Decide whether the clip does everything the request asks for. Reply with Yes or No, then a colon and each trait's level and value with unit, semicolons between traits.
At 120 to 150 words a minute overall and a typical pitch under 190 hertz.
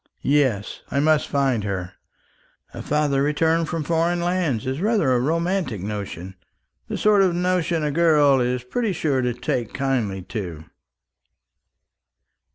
Yes: average, 140 wpm; medium, 140 Hz